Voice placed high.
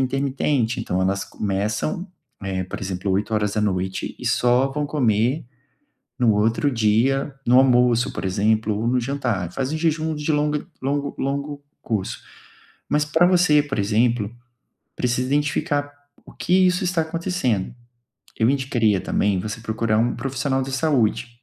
No: low, 125 Hz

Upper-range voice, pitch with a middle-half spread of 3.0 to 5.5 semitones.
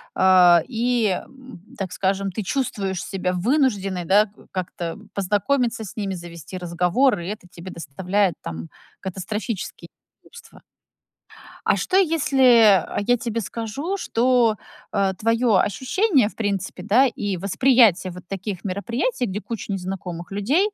Yes: high, 205 Hz; average, 4.7 semitones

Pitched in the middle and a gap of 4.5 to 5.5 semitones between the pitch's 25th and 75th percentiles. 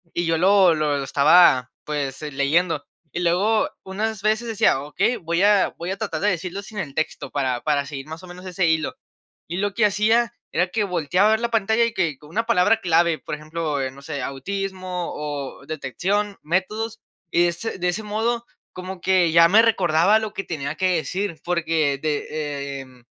Yes: medium, 175 Hz; average, 5.0 semitones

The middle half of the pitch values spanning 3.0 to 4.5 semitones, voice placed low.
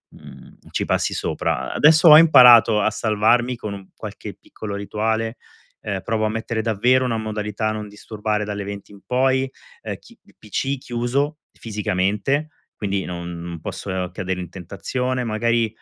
Yes: average, 3.4 semitones; low, 110 Hz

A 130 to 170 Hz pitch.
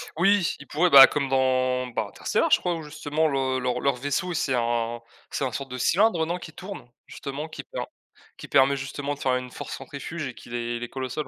Yes: low, 135 Hz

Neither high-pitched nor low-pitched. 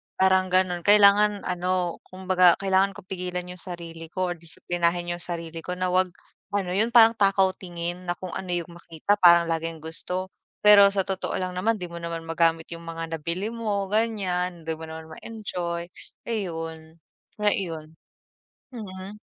Yes: medium, 180 Hz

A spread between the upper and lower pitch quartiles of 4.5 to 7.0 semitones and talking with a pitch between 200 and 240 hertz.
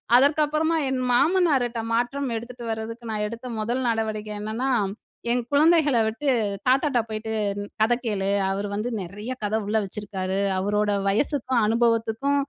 No: average, 3.7 semitones; high, 230 Hz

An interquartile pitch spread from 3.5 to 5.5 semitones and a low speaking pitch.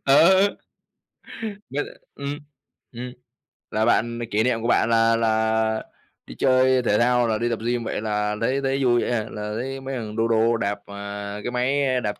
No: average, 2.7 semitones; low, 115 Hz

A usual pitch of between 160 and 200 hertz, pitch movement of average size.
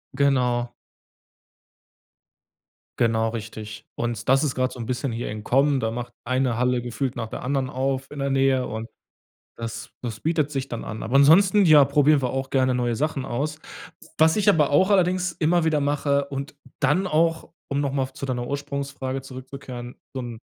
No: low, 135 Hz; average, 3.0 semitones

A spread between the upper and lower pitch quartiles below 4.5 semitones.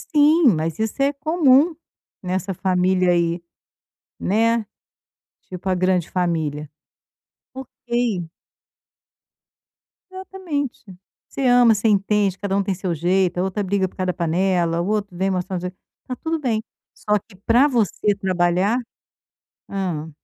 No: average, 4.8 semitones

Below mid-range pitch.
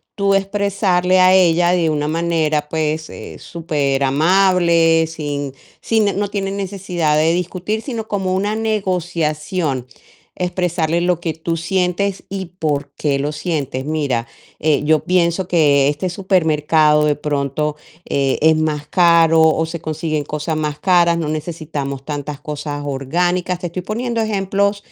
No: medium, 165 Hz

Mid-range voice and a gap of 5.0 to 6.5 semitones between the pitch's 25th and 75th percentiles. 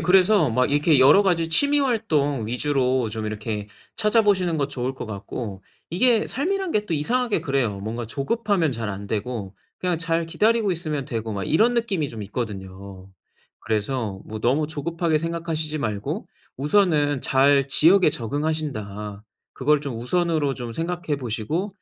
No: medium, 145 Hz; wide, 7.3 semitones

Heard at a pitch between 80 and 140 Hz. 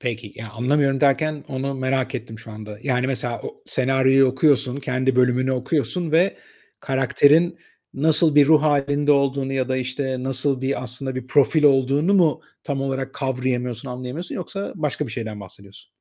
Yes: low, 135 Hz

